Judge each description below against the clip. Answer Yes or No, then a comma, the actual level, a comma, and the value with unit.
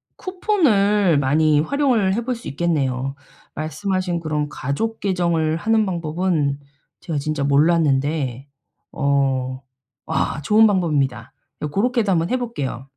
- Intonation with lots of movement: Yes, wide, 6.2 semitones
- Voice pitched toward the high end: No, medium, 160 Hz